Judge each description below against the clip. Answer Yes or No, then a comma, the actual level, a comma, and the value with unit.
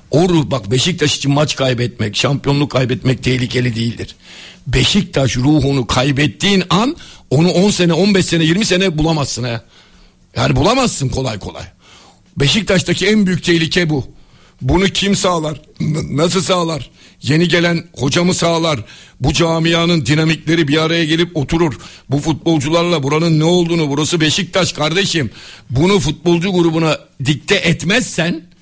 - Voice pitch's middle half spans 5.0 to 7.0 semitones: No, average, 4.4 semitones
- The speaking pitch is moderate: Yes, medium, 160 Hz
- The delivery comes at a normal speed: Yes, average, 130 wpm